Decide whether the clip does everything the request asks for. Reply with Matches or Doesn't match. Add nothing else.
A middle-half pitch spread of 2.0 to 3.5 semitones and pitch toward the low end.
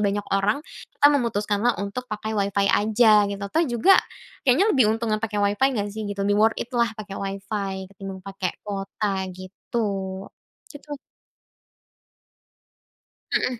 Doesn't match